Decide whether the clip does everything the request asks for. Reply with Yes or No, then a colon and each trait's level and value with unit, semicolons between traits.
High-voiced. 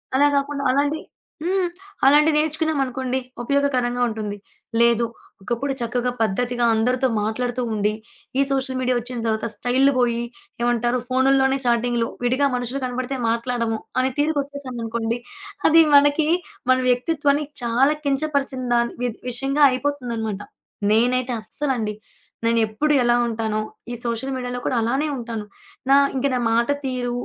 Yes: very high, 250 Hz